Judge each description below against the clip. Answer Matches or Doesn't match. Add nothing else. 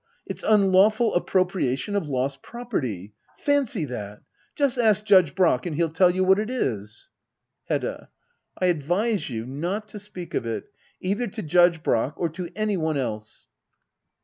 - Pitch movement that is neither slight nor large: Doesn't match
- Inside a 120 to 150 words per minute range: Doesn't match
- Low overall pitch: Doesn't match